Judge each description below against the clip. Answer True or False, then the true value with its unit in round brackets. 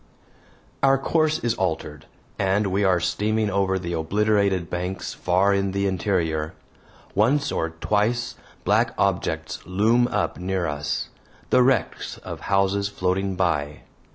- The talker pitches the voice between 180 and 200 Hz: False (95 Hz)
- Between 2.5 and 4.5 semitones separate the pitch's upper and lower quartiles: True (2.9 semitones)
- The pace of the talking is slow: True (130 wpm)